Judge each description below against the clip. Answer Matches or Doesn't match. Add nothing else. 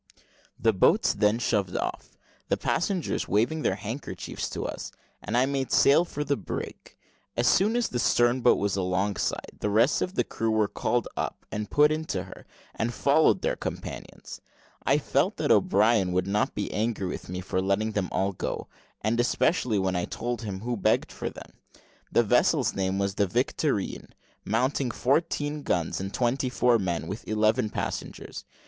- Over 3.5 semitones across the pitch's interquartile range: Matches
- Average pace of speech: Matches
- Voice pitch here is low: Matches